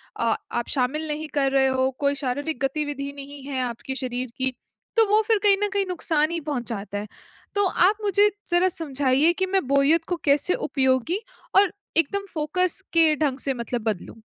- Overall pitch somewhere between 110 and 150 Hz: No, very high, 285 Hz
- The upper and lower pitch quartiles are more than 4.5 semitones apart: Yes, average, 5.0 semitones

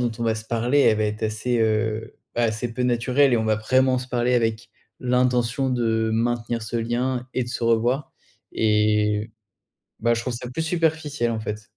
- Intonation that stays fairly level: Yes, narrow, 2.1 semitones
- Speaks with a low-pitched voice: Yes, low, 120 Hz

